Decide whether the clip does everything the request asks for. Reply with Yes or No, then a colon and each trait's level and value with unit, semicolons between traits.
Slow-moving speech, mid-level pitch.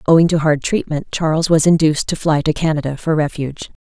No: fast, 205 wpm; medium, 155 Hz